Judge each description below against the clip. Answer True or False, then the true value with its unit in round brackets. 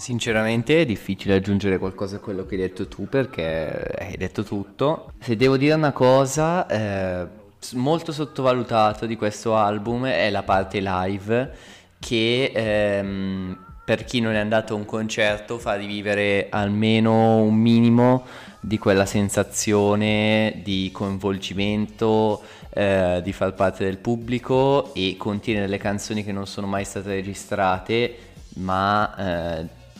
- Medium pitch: False (105 Hz)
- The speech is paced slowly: False (135 wpm)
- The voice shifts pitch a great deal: False (2.8 semitones)